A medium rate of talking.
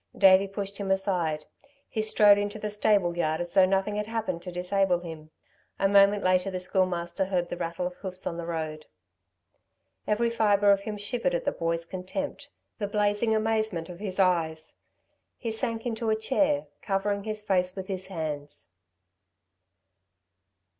Yes: average, 165 wpm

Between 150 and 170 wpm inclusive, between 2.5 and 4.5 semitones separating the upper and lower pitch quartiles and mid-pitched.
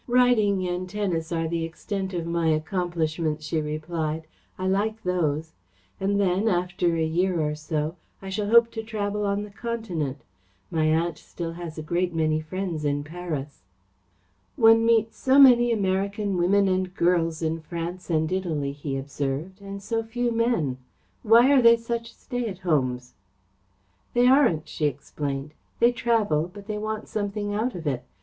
No: average, 165 wpm; average, 4.9 semitones; medium, 180 Hz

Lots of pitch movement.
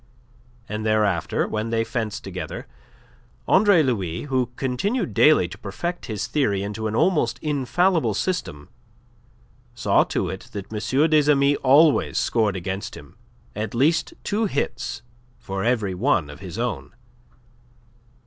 Yes: wide, 6.6 semitones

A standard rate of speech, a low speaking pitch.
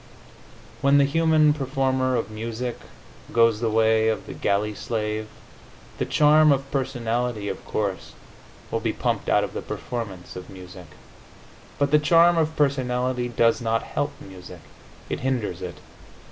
Yes: average, 145 wpm; low, 120 Hz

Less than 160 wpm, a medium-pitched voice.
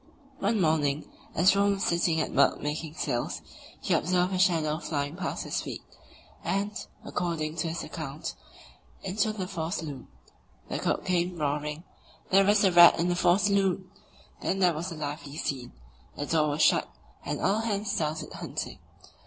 No: average, 165 wpm; medium, 170 Hz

